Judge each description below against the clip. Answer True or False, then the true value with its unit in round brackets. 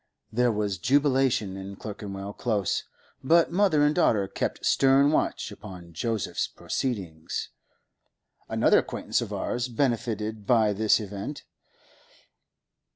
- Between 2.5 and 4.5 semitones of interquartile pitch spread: False (5.2 semitones)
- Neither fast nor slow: False (110 wpm)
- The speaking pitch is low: True (110 Hz)